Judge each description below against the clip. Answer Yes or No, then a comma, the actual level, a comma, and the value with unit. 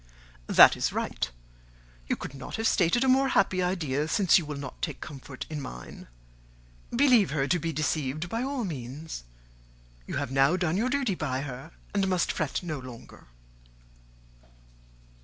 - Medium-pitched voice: Yes, medium, 160 Hz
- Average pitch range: No, wide, 5.8 semitones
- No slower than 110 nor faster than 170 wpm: Yes, average, 160 wpm